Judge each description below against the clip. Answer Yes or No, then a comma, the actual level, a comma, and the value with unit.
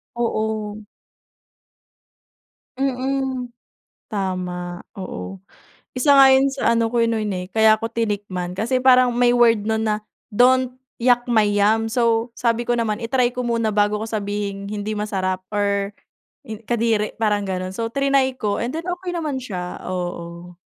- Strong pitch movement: No, average, 3.3 semitones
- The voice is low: No, high, 220 Hz